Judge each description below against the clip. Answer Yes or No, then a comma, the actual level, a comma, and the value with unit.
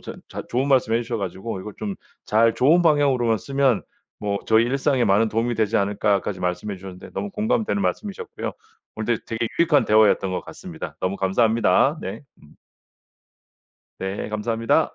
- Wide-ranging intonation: No, average, 4.9 semitones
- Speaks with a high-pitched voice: No, low, 115 Hz